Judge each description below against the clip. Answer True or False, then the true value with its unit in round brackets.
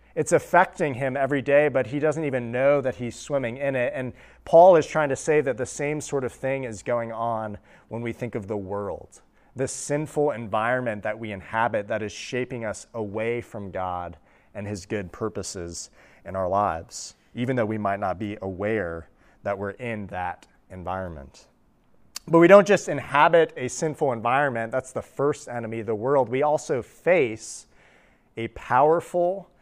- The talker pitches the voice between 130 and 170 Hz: False (120 Hz)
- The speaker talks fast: False (180 wpm)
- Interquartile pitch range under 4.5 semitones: False (5.3 semitones)